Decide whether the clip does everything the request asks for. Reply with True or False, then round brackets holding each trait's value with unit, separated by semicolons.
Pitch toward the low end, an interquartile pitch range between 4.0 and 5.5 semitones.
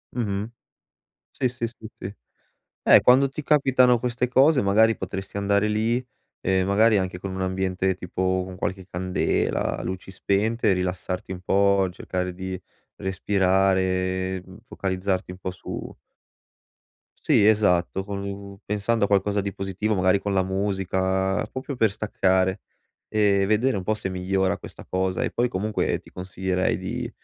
False (95 Hz; 2.4 semitones)